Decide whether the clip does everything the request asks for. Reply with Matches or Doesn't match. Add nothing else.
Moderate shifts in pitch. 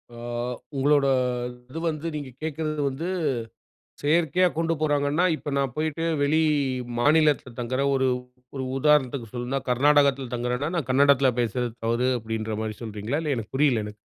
Matches